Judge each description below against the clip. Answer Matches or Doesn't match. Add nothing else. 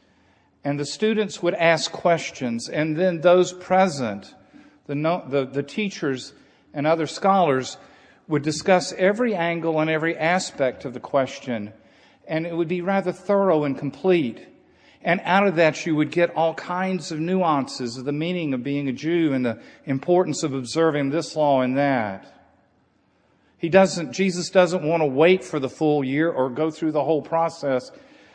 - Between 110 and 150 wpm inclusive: Doesn't match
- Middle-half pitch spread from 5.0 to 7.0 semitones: Doesn't match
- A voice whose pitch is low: Doesn't match